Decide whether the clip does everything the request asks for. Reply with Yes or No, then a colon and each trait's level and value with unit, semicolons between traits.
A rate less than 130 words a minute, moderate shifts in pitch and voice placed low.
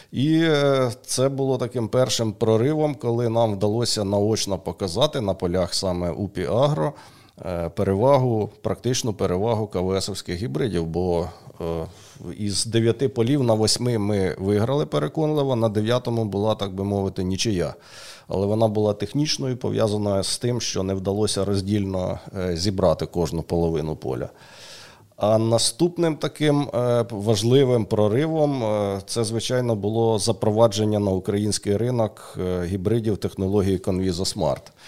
Yes: average, 115 wpm; average, 3.8 semitones; low, 105 Hz